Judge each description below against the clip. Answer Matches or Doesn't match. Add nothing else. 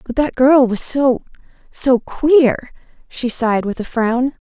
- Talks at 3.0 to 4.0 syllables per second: Matches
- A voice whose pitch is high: Matches